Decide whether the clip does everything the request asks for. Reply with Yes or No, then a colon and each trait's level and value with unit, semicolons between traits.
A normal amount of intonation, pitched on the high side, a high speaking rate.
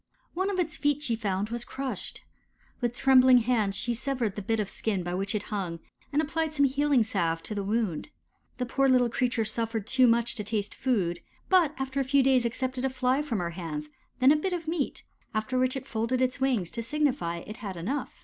Yes: average, 4.4 semitones; high, 245 Hz; fast, 215 wpm